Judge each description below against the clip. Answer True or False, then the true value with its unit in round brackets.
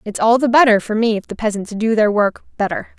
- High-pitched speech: True (220 Hz)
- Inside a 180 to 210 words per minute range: False (260 wpm)